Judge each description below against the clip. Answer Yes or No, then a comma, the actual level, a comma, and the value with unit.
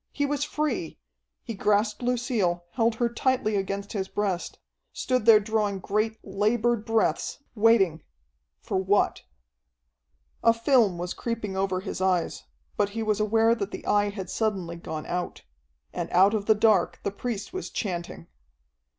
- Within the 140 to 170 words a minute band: Yes, average, 150 wpm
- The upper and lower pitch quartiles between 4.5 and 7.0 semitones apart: No, average, 3.1 semitones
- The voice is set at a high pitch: Yes, high, 210 Hz